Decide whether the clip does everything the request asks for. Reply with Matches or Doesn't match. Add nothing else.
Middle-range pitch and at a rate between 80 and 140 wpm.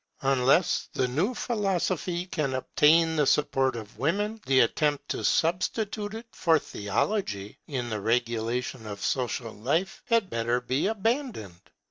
Matches